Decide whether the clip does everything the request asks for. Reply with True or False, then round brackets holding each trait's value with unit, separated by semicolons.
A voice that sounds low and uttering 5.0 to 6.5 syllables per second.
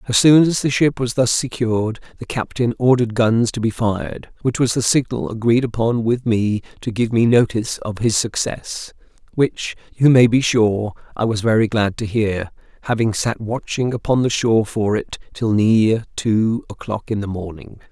False (115 Hz; 4.8 syllables/s)